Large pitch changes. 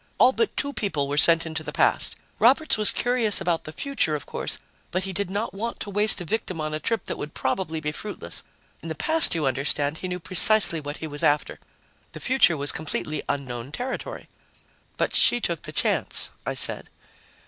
Yes: wide, 6.2 semitones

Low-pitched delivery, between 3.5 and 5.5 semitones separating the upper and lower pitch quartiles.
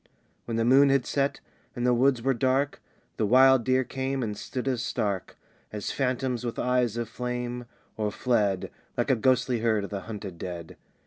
No: low, 125 Hz; average, 3.0 semitones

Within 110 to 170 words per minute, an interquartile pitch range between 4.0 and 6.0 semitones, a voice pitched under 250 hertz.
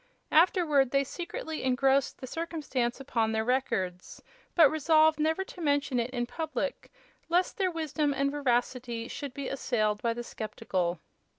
No: average, 150 wpm; average, 4.6 semitones; very high, 275 Hz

